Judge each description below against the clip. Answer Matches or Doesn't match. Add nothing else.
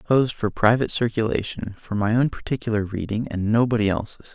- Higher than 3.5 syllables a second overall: Matches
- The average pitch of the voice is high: Doesn't match